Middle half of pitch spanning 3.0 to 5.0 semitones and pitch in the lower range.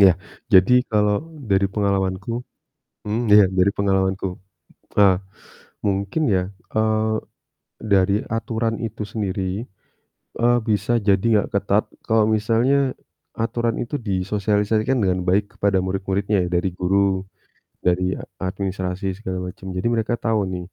No: narrow, 2.4 semitones; low, 100 Hz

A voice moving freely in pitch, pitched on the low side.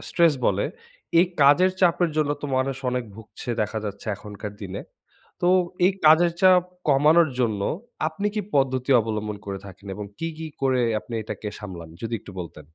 Yes: wide, 7.4 semitones; low, 130 Hz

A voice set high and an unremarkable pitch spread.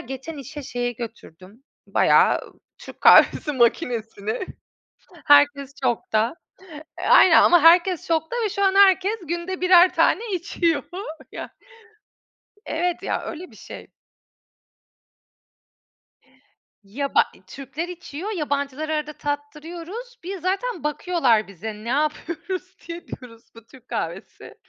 No: very high, 300 Hz; wide, 6.0 semitones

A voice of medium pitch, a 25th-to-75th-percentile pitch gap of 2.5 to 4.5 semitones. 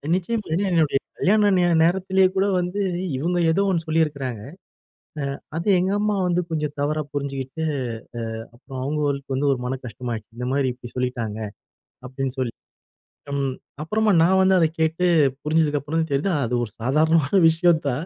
No: medium, 155 Hz; average, 4.9 semitones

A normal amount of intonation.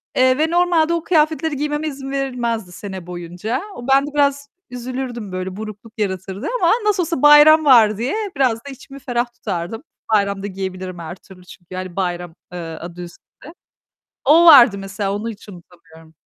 No: wide, 7.1 semitones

